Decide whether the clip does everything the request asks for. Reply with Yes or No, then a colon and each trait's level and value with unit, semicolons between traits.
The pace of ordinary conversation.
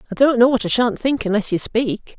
No: fast, 275 wpm